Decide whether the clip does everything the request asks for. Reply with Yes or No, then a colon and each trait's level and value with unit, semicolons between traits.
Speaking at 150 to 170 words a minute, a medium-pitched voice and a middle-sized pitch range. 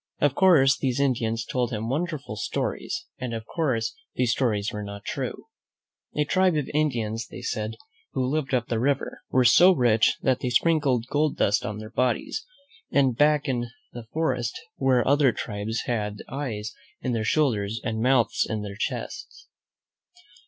No: average, 165 wpm; low, 125 Hz; average, 4.2 semitones